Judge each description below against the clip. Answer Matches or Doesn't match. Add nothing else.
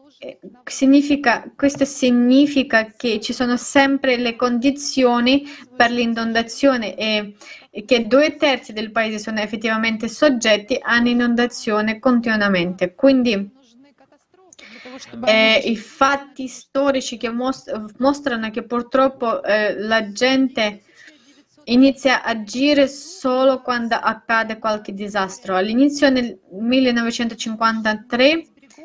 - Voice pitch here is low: Doesn't match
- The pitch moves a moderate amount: Matches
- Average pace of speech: Doesn't match